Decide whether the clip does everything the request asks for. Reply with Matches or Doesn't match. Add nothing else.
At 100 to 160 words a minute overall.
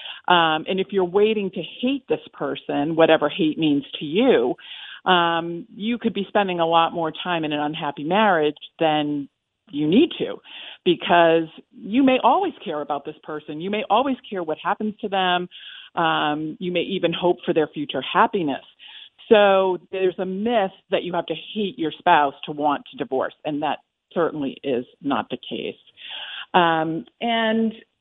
Doesn't match